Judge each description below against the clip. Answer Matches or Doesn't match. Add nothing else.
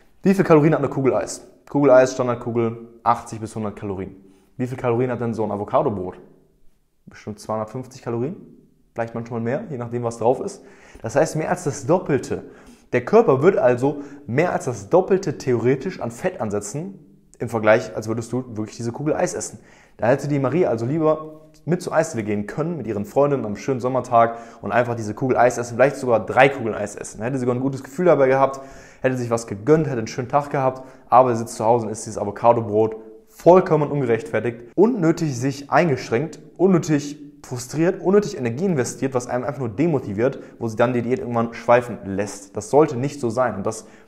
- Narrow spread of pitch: Doesn't match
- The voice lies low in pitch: Matches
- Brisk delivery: Matches